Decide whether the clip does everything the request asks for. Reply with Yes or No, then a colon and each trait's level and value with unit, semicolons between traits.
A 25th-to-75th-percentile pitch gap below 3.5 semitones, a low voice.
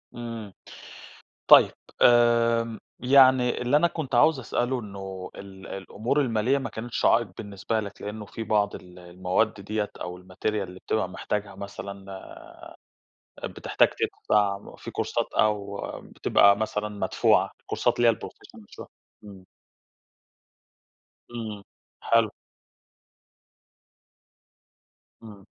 Yes: average, 2.9 semitones; low, 105 Hz